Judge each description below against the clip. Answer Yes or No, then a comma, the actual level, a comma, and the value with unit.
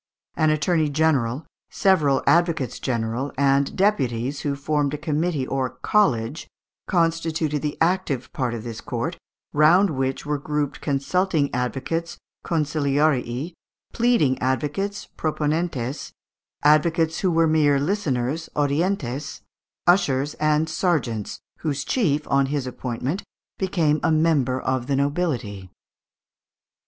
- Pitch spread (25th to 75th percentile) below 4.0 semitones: Yes, average, 3.6 semitones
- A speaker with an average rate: No, slow, 115 wpm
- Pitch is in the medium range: Yes, medium, 150 Hz